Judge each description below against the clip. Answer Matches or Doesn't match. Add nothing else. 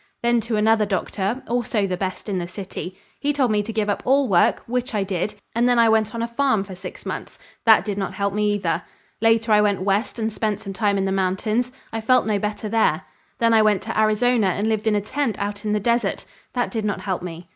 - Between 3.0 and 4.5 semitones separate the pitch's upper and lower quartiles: Doesn't match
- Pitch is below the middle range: Doesn't match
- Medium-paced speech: Doesn't match